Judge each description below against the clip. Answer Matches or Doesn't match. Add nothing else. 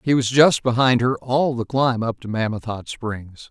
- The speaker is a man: Matches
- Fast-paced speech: Matches